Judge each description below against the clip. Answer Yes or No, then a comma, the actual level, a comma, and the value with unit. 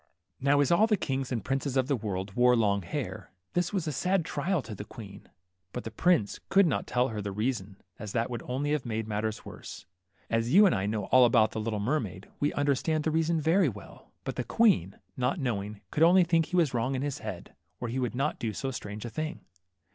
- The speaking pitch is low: Yes, low, 125 Hz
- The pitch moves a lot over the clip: Yes, wide, 6.2 semitones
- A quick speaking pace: Yes, fast, 235 wpm